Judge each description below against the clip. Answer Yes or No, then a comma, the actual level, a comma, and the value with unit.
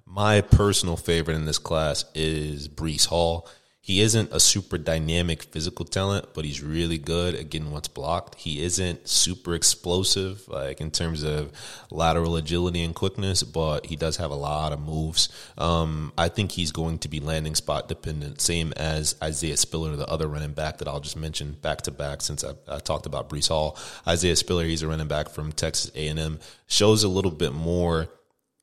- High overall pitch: No, very low, 80 Hz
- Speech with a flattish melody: Yes, narrow, 2.3 semitones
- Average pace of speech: Yes, average, 190 wpm